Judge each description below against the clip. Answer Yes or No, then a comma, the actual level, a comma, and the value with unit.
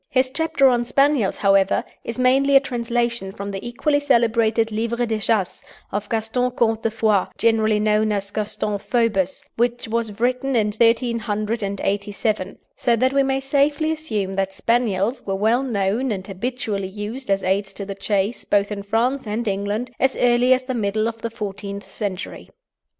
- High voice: Yes, high, 225 Hz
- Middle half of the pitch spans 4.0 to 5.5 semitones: No, average, 3.4 semitones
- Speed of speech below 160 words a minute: No, average, 165 wpm